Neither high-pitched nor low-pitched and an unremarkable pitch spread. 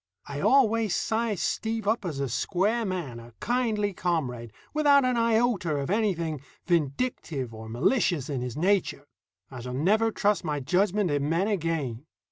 No: medium, 180 Hz; wide, 7.8 semitones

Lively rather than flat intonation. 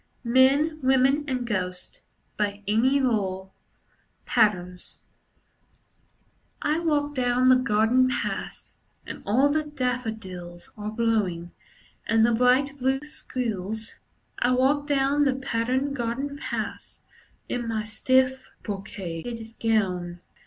No: average, 4.1 semitones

